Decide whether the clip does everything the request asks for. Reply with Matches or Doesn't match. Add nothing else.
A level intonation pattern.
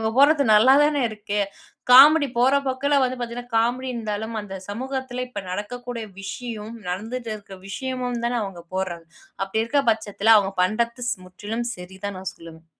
Doesn't match